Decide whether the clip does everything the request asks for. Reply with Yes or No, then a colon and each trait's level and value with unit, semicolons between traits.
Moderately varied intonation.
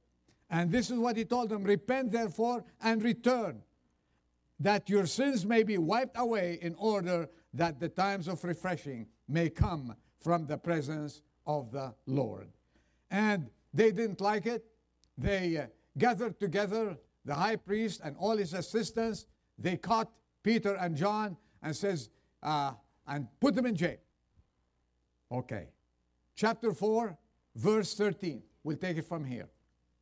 No: wide, 7.8 semitones